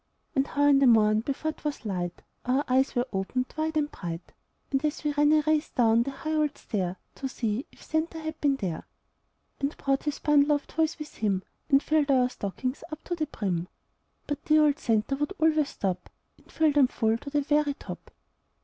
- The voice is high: Yes, very high, 280 Hz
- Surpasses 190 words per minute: Yes, fast, 205 wpm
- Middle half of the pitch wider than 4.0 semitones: Yes, average, 4.9 semitones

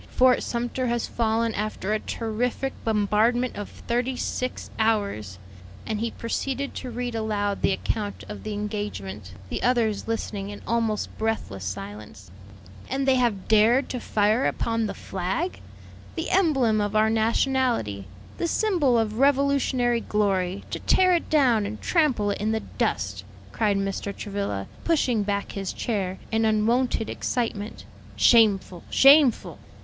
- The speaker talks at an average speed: Yes, average, 145 wpm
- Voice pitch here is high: Yes, high, 220 Hz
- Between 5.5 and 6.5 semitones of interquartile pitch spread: No, average, 3.5 semitones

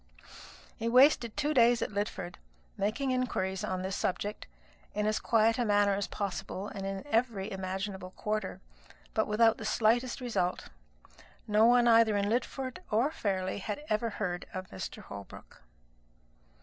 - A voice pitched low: No, high, 210 Hz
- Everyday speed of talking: Yes, average, 150 wpm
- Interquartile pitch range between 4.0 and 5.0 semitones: No, average, 3.4 semitones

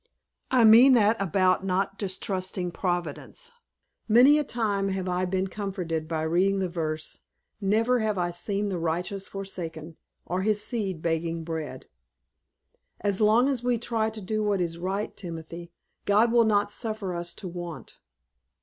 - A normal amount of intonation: Yes, average, 3.9 semitones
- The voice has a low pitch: No, high, 190 Hz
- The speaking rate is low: No, average, 155 wpm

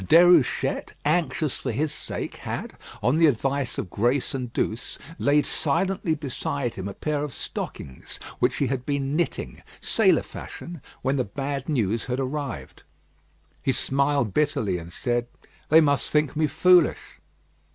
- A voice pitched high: No, medium, 140 Hz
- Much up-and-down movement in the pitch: No, average, 3.7 semitones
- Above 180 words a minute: No, average, 150 wpm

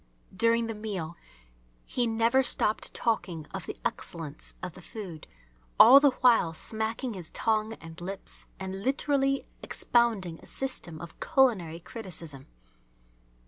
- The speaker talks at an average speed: No, slow, 130 wpm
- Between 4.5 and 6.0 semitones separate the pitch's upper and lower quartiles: Yes, wide, 5.6 semitones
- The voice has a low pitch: No, high, 215 Hz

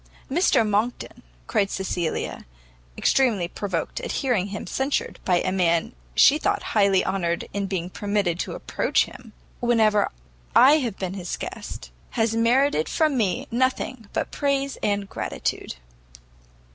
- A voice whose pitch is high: Yes, high, 205 Hz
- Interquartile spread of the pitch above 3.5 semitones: Yes, average, 5.0 semitones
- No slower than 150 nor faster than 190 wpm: No, slow, 135 wpm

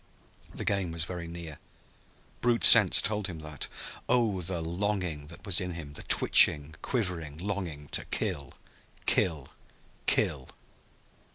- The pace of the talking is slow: Yes, slow, 130 wpm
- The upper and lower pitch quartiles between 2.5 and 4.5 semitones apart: Yes, average, 4.2 semitones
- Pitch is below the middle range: Yes, very low, 85 Hz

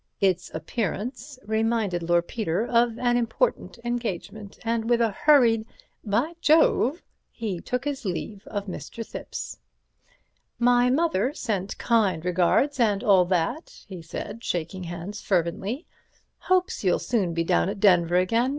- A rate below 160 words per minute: Yes, average, 140 wpm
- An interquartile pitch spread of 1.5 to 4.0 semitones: No, average, 4.9 semitones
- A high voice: Yes, high, 215 Hz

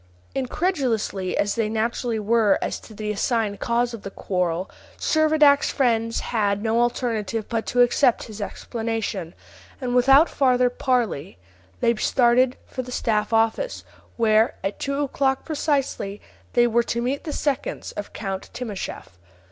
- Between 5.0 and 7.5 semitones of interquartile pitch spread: No, average, 3.2 semitones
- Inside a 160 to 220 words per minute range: No, average, 145 wpm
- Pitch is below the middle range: No, high, 235 Hz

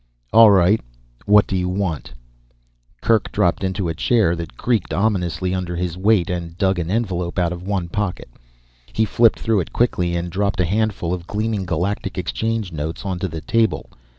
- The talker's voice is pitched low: Yes, very low, 95 Hz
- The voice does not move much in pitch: No, average, 3.2 semitones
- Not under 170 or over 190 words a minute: Yes, average, 180 wpm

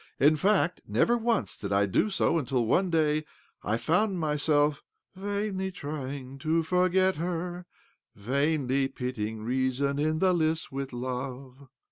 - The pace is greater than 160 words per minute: No, average, 140 wpm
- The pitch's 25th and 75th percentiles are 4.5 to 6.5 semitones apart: Yes, wide, 5.5 semitones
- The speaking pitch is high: No, medium, 150 Hz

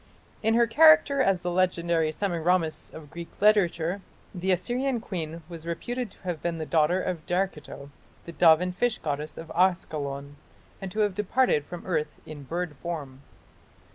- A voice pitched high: No, medium, 175 Hz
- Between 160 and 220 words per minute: Yes, average, 165 wpm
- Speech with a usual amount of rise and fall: Yes, average, 3.6 semitones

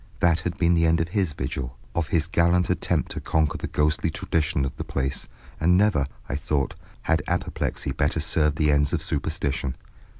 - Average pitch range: Yes, average, 3.0 semitones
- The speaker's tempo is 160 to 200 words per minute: Yes, average, 190 wpm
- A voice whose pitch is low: Yes, very low, 80 Hz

